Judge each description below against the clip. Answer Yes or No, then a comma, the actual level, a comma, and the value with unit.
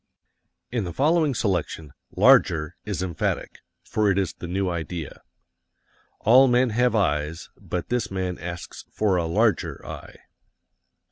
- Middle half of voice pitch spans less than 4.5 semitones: No, average, 4.9 semitones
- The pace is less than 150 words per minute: Yes, slow, 135 wpm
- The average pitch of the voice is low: Yes, very low, 95 Hz